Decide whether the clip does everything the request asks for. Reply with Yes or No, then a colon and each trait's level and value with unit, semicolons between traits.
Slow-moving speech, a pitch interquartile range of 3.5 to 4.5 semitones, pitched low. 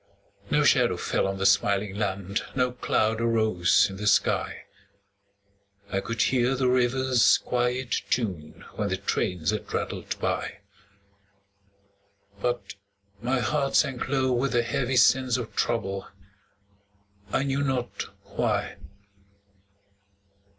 Yes: slow, 120 wpm; average, 4.0 semitones; low, 120 Hz